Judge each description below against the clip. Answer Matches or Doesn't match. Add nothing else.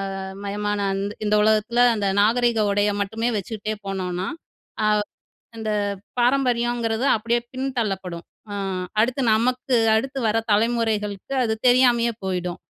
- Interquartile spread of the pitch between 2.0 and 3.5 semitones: Matches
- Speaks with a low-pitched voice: Doesn't match